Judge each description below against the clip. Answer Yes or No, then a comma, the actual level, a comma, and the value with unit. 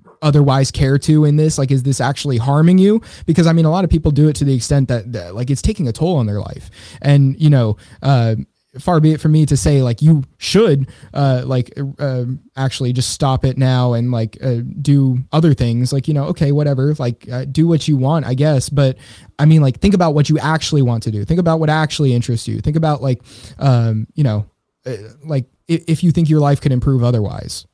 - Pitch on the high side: No, medium, 140 Hz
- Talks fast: Yes, fast, 235 wpm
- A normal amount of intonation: Yes, average, 3.6 semitones